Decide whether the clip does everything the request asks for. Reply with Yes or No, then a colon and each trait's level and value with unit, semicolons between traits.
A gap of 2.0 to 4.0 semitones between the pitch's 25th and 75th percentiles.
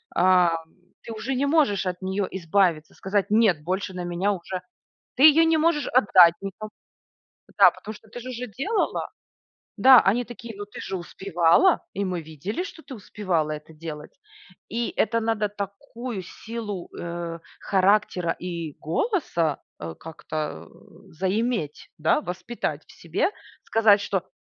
No: average, 5.0 semitones